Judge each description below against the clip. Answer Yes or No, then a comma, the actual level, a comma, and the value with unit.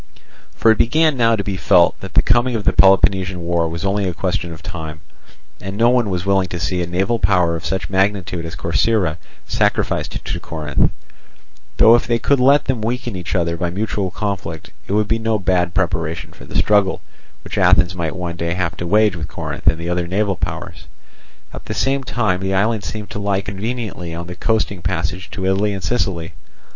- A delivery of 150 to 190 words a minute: No, fast, 205 wpm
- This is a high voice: No, very low, 95 Hz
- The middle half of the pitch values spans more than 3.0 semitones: Yes, average, 3.7 semitones